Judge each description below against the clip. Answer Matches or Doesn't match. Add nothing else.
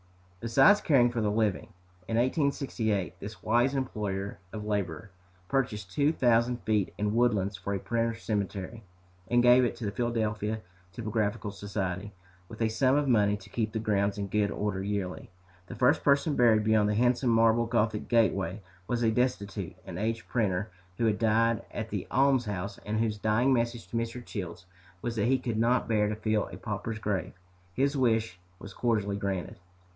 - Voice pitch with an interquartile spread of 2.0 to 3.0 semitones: Matches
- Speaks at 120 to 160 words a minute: Doesn't match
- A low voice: Matches